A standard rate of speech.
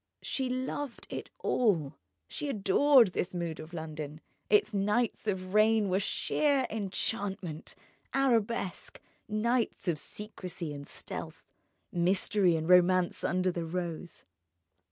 No: slow, 115 wpm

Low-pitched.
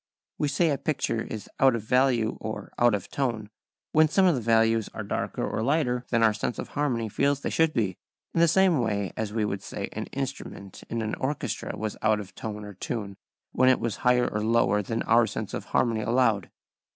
Yes: low, 115 Hz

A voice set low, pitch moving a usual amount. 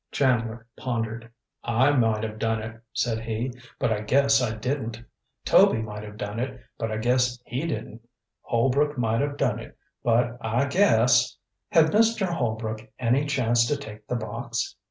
Yes: low, 115 Hz; average, 3.0 semitones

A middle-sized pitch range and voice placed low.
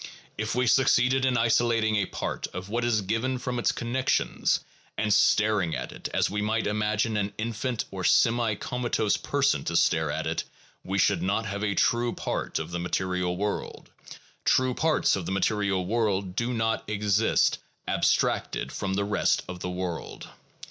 Yes: average, 3.4 semitones; low, 105 Hz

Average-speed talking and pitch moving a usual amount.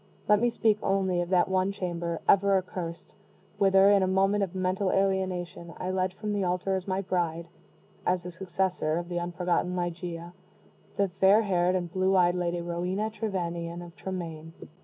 No: average, 175 wpm; narrow, 1.8 semitones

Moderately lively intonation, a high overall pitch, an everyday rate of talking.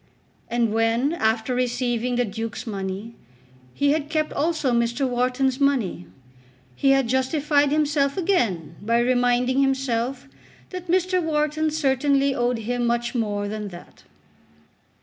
No: average, 3.6 semitones; very high, 250 Hz; slow, 130 wpm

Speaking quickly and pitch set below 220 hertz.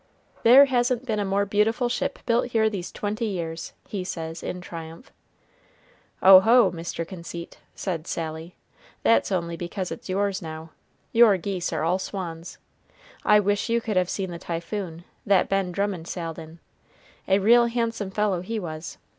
No: average, 160 wpm; high, 190 Hz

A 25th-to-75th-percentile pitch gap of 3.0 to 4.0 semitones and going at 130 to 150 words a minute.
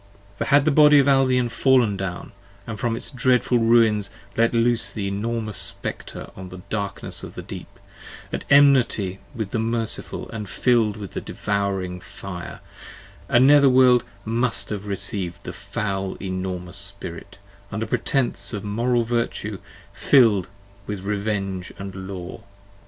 Yes: average, 3.7 semitones; average, 145 wpm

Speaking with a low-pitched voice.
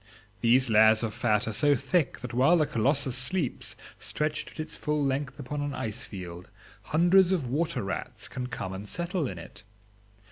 Yes: low, 130 Hz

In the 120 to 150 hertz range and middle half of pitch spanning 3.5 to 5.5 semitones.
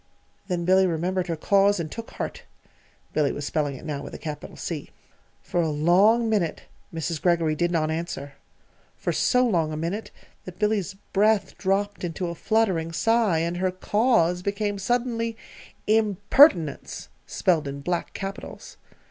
No: medium, 180 Hz; average, 4.1 semitones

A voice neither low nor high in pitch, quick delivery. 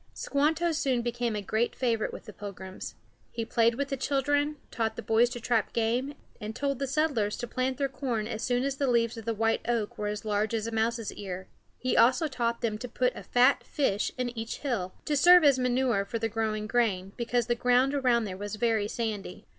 No: high, 235 Hz; fast, 220 wpm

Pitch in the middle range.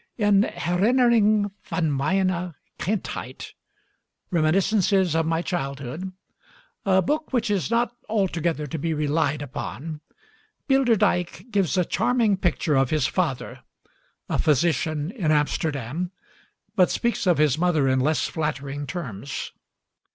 Yes: medium, 170 Hz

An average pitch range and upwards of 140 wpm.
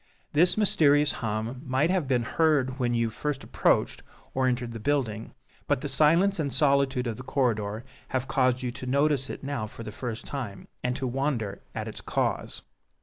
Yes: average, 3.4 semitones; average, 185 wpm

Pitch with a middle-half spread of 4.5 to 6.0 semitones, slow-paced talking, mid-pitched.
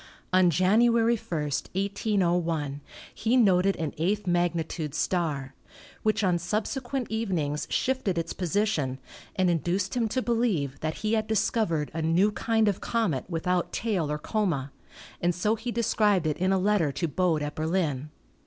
No: average, 5.1 semitones; average, 160 wpm; medium, 180 Hz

